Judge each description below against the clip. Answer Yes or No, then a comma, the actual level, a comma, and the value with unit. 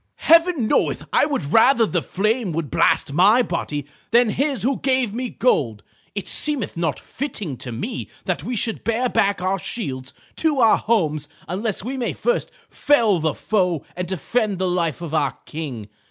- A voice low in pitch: No, high, 200 Hz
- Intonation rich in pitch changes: Yes, wide, 7.1 semitones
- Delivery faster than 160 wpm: Yes, average, 175 wpm